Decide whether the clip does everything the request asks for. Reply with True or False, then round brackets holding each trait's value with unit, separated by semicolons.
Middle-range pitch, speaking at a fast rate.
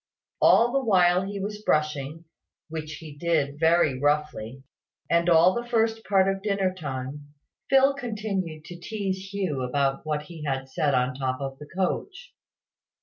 False (165 Hz; 160 wpm)